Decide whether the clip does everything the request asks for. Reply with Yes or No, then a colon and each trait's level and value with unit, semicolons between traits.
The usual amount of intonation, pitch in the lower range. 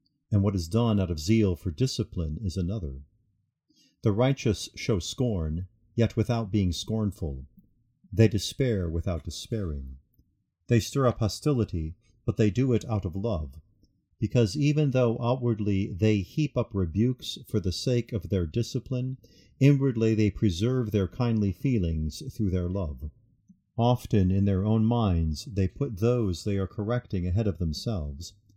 Yes: average, 4.0 semitones; low, 105 Hz